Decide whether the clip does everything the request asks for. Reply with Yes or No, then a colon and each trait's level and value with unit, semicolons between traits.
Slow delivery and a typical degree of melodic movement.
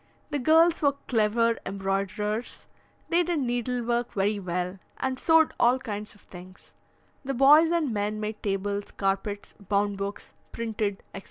No: average, 150 wpm; average, 4.5 semitones